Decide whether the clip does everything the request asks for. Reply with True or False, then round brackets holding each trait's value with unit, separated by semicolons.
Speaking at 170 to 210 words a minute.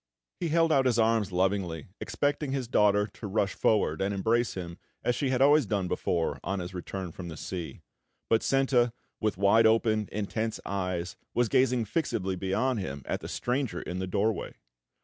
True (175 wpm)